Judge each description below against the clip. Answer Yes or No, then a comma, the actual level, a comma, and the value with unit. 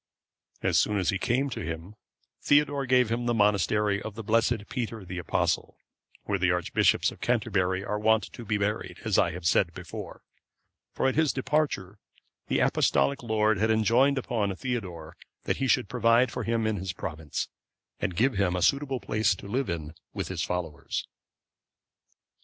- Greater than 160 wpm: Yes, average, 175 wpm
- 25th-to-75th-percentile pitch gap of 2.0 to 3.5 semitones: No, average, 4.6 semitones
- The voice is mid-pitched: No, low, 105 Hz